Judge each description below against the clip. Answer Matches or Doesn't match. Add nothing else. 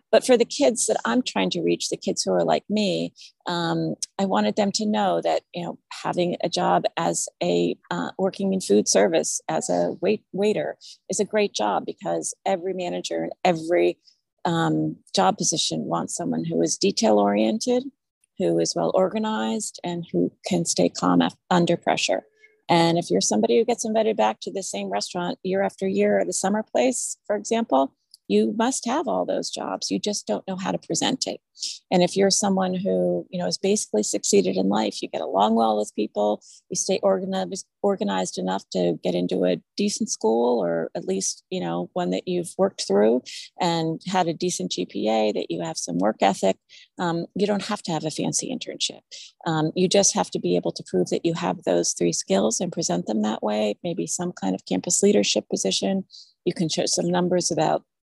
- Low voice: Doesn't match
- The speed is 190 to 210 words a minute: Matches